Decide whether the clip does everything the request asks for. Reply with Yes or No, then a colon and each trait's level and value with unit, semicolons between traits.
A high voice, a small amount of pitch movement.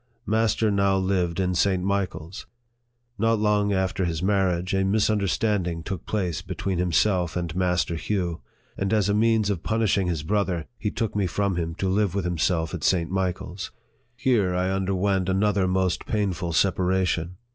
No: very low, 95 Hz; narrow, 2.3 semitones